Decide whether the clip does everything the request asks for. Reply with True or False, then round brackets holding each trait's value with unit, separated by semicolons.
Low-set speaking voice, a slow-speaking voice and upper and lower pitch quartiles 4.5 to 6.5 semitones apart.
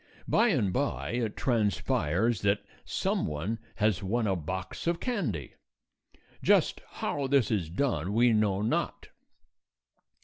True (110 Hz; 130 wpm; 4.8 semitones)